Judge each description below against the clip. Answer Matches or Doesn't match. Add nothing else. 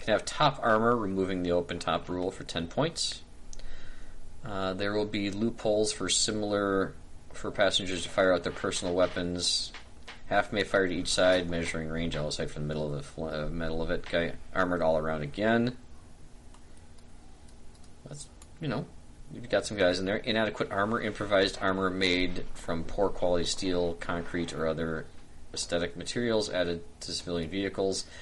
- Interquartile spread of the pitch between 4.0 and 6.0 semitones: Doesn't match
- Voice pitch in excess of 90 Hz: Doesn't match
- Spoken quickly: Doesn't match